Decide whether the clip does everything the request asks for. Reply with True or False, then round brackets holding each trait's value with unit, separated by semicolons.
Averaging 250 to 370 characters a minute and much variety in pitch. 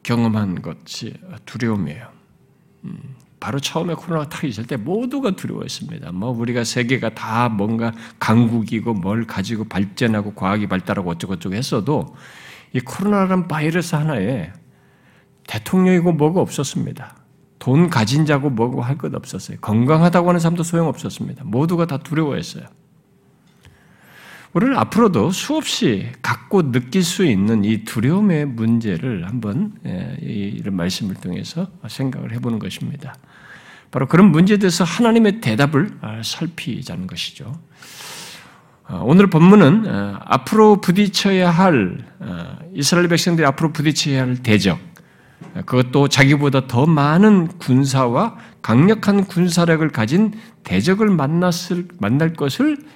True (300 characters per minute; 7.1 semitones)